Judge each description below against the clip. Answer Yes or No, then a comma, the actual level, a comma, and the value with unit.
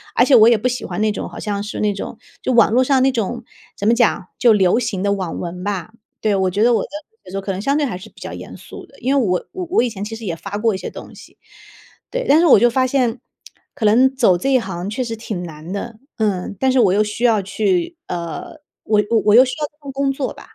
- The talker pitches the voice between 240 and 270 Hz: No, high, 220 Hz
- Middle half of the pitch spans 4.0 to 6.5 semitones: Yes, average, 4.6 semitones